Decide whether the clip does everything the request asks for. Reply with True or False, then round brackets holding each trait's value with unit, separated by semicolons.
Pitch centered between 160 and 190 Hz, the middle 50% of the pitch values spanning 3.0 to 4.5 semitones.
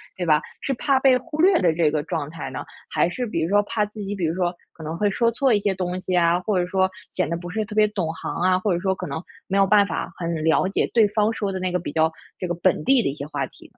True (185 Hz; 3.8 semitones)